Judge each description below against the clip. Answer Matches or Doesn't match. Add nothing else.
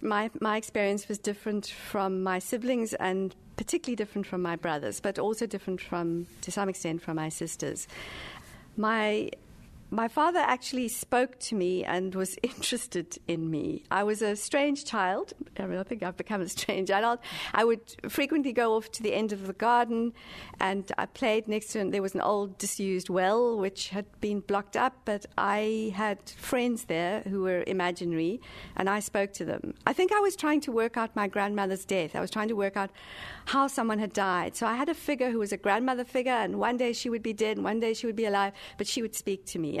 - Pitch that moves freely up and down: Doesn't match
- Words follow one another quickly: Matches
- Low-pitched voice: Doesn't match